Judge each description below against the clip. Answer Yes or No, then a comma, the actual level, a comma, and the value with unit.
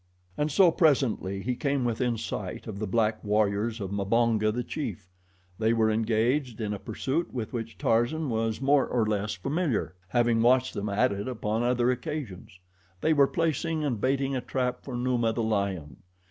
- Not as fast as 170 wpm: No, average, 175 wpm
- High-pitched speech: No, low, 115 Hz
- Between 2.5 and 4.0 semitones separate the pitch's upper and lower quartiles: Yes, average, 3.5 semitones